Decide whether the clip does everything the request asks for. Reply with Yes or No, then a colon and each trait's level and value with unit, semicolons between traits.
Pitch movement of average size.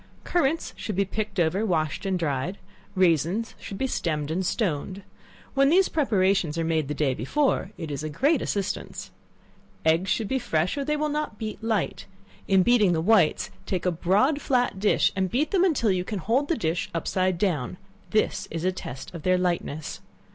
No: wide, 5.9 semitones